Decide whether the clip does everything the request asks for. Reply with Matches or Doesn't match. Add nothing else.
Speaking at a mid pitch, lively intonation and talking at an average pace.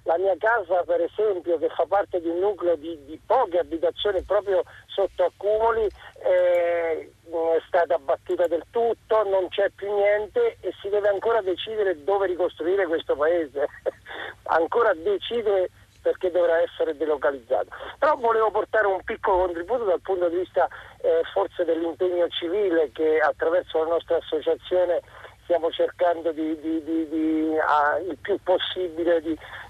Doesn't match